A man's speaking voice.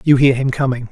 Yes: male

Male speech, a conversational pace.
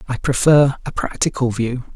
Yes: male; average, 155 wpm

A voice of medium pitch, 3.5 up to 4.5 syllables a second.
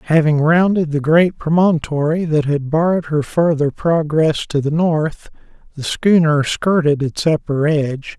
Yes: medium, 155 Hz; 4.3 syllables/s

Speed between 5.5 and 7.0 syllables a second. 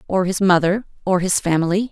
Yes: 5.8 syllables/s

